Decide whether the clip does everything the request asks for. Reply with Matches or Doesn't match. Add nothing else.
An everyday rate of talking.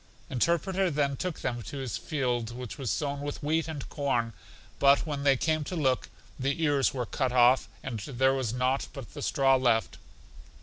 Matches